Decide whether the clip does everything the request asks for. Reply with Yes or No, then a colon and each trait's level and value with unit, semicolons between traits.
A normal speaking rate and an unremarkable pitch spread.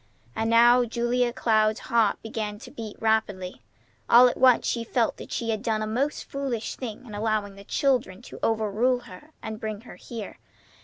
No: average, 185 wpm; narrow, 2.0 semitones